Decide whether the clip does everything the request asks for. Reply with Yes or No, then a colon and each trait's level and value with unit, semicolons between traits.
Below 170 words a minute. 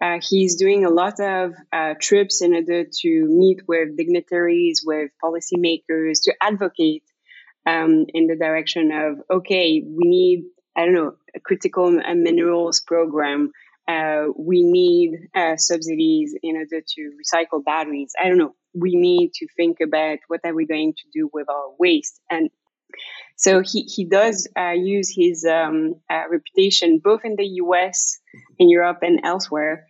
Yes: average, 160 wpm